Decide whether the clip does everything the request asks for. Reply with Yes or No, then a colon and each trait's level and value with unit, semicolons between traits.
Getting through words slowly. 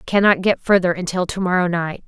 No: fast, 205 wpm